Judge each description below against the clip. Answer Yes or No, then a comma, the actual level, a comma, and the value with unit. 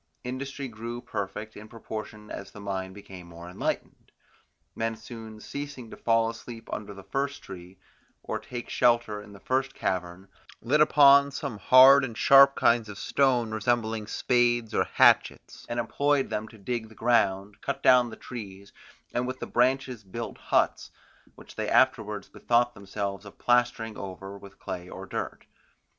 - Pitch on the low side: Yes, low, 115 Hz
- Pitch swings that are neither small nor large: Yes, average, 3.6 semitones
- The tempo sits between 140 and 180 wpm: Yes, average, 160 wpm